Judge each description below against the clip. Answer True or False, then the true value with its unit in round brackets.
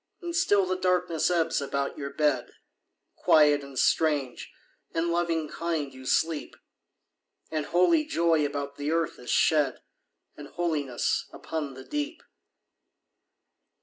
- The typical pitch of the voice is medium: True (160 Hz)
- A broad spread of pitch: False (3.4 semitones)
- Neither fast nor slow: False (125 wpm)